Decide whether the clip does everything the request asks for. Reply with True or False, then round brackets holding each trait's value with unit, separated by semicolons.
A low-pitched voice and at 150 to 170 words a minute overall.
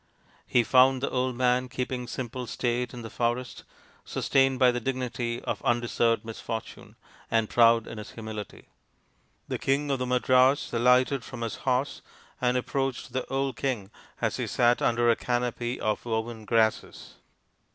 True (125 Hz; 155 wpm)